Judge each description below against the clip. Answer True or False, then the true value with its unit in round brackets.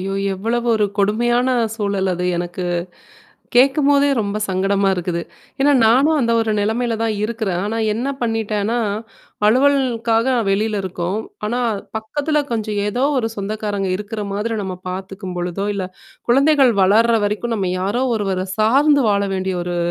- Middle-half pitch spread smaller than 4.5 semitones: True (3.5 semitones)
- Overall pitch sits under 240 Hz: True (215 Hz)